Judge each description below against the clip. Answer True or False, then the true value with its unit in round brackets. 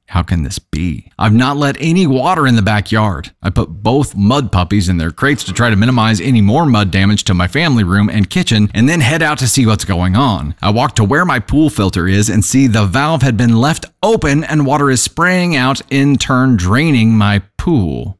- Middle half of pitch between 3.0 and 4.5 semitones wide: False (5.5 semitones)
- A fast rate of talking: True (225 wpm)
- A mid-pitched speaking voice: False (115 Hz)